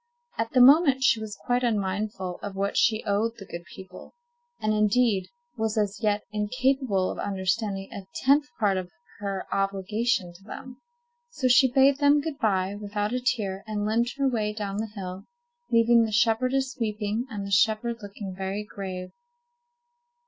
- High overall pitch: Yes, high, 215 Hz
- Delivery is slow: No, average, 165 wpm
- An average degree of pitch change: Yes, average, 3.6 semitones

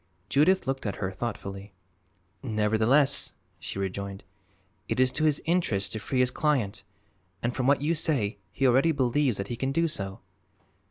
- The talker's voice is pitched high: No, low, 125 Hz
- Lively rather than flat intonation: Yes, wide, 6.0 semitones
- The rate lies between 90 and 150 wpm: No, average, 165 wpm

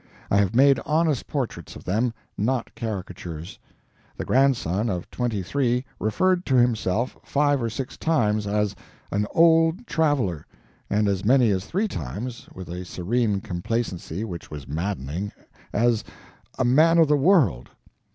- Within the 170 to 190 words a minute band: No, average, 145 wpm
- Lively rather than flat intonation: Yes, wide, 6.3 semitones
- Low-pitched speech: Yes, low, 115 Hz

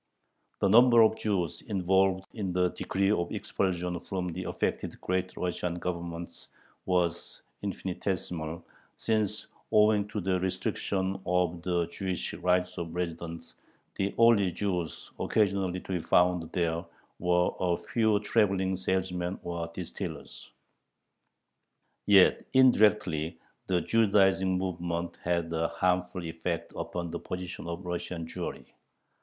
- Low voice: Yes, very low, 90 Hz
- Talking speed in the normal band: No, slow, 120 wpm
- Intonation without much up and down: Yes, narrow, 2.0 semitones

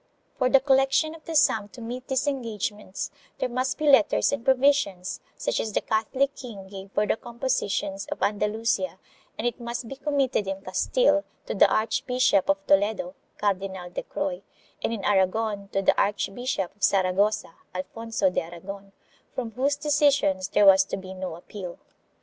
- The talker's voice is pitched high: Yes, high, 215 Hz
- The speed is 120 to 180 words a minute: Yes, average, 165 wpm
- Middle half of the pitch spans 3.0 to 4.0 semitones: No, average, 5.1 semitones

